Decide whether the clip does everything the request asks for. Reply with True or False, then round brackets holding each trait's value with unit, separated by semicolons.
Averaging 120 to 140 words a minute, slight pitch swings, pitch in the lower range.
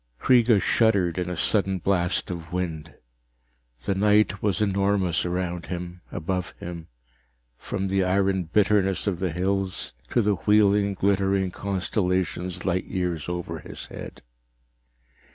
True (135 wpm; 2.1 semitones; 95 Hz)